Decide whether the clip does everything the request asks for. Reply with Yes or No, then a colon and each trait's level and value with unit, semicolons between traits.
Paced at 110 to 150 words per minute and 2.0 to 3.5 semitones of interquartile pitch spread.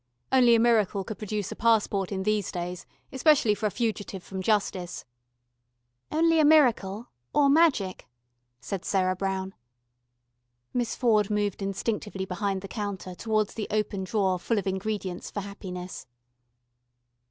Yes: average, 140 wpm; average, 2.9 semitones